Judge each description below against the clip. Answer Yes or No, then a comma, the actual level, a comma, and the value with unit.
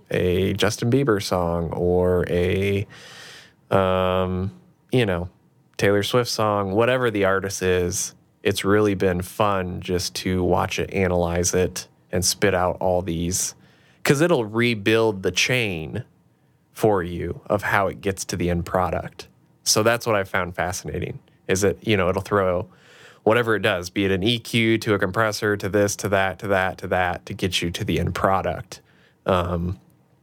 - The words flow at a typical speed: Yes, average, 165 wpm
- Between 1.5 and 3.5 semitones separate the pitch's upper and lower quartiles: Yes, average, 2.8 semitones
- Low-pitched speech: Yes, very low, 95 Hz